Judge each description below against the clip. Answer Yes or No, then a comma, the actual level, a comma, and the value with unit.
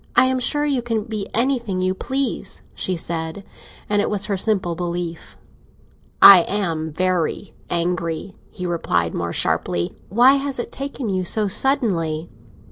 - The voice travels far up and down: Yes, wide, 5.8 semitones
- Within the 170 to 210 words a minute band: No, average, 150 wpm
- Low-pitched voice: No, high, 190 Hz